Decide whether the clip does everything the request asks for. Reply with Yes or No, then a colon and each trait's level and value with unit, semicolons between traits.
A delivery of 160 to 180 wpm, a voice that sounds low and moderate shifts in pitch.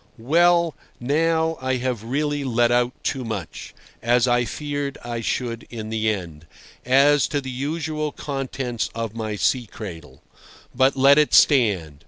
No: average, 150 wpm; low, 125 Hz; average, 4.1 semitones